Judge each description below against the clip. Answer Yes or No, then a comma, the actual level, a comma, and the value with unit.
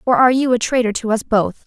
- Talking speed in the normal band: No, fast, 290 wpm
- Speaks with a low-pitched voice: No, high, 235 Hz